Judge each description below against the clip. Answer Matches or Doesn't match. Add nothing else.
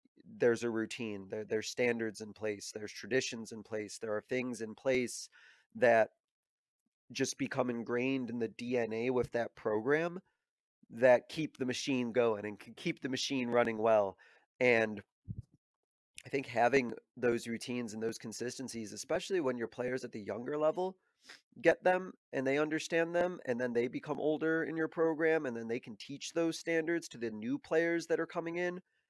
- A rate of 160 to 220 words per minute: Matches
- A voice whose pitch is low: Matches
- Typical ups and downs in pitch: Doesn't match